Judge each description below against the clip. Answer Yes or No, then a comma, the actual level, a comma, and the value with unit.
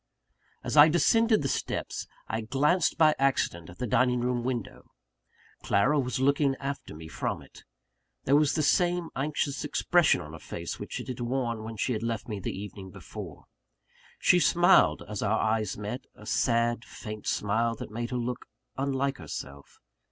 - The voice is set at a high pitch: No, low, 125 Hz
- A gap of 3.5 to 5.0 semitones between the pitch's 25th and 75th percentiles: Yes, average, 4.4 semitones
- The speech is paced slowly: No, average, 170 wpm